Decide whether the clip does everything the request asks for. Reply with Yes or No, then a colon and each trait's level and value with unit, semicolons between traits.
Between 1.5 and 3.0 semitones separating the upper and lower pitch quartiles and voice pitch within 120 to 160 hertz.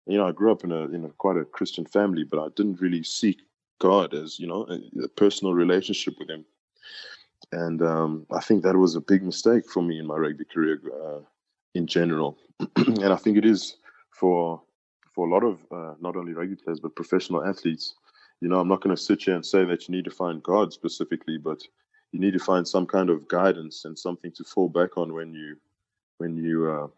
No: average, 2.7 semitones; very low, 90 Hz